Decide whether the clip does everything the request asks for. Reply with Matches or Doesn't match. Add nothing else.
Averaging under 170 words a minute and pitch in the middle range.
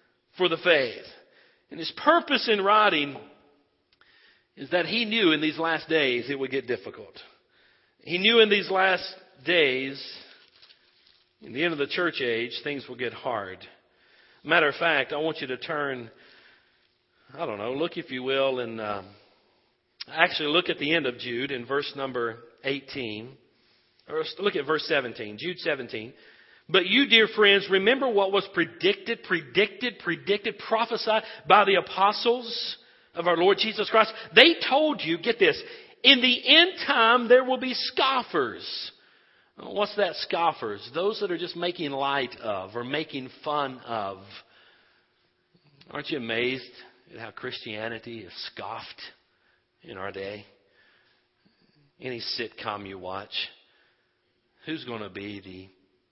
Matches